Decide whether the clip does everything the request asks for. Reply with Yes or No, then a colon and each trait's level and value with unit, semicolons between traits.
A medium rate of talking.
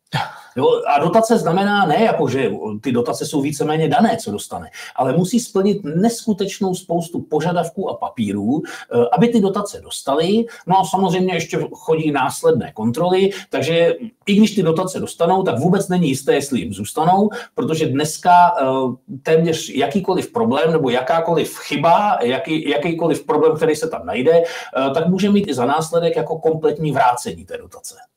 Yes: average, 150 wpm